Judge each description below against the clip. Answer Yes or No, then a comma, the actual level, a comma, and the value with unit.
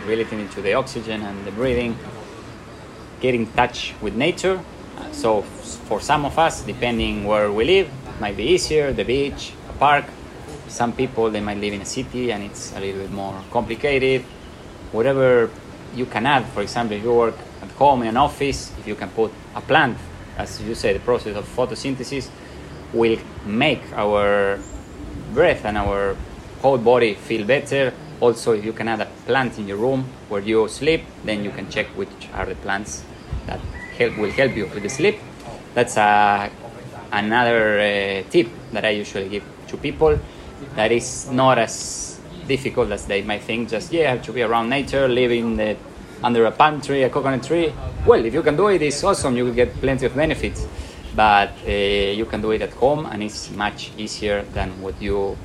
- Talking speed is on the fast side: No, average, 185 wpm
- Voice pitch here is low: Yes, low, 115 Hz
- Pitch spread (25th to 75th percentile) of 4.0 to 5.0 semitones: Yes, average, 4.3 semitones